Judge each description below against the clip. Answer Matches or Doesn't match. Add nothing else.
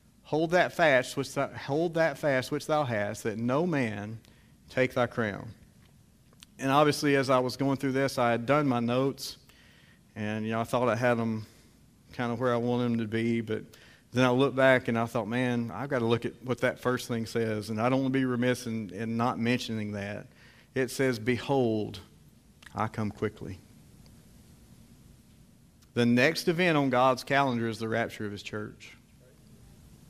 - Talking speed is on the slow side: Doesn't match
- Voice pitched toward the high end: Doesn't match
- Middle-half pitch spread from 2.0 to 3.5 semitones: Matches